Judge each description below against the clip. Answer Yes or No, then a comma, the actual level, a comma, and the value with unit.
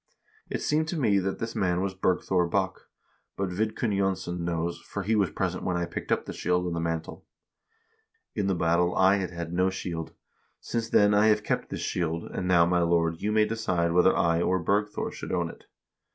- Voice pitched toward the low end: Yes, very low, 90 Hz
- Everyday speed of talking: No, fast, 210 wpm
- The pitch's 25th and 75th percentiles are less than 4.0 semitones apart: Yes, average, 3.1 semitones